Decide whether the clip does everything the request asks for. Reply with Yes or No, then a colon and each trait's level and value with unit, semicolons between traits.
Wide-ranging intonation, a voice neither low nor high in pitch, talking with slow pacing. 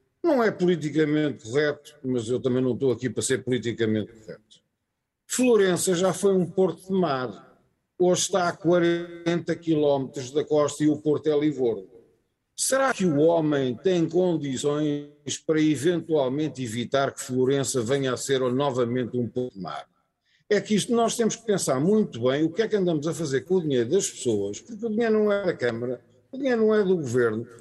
No: wide, 6.1 semitones; medium, 150 Hz; fast, 185 wpm